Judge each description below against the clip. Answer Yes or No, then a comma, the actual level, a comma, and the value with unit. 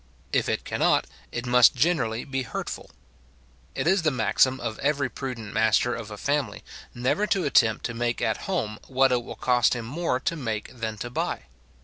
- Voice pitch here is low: Yes, low, 125 Hz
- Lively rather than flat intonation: No, average, 3.5 semitones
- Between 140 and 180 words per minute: No, average, 190 wpm